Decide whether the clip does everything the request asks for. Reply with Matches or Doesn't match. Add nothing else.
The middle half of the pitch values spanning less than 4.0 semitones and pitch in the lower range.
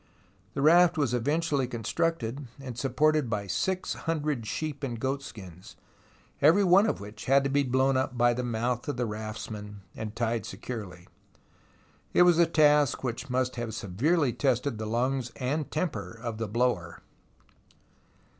Doesn't match